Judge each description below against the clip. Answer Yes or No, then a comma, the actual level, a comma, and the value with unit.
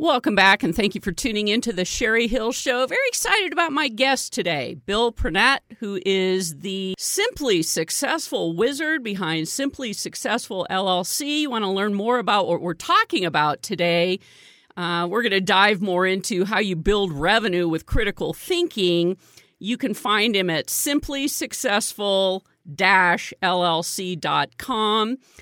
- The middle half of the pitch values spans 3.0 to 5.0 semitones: No, wide, 5.6 semitones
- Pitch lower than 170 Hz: No, high, 205 Hz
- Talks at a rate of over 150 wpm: No, average, 145 wpm